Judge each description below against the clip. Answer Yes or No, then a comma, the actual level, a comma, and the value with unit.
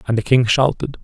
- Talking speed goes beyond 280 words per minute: No, fast, 230 wpm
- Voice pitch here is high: No, low, 125 Hz